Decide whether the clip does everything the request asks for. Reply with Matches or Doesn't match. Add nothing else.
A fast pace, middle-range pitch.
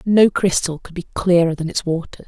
Matches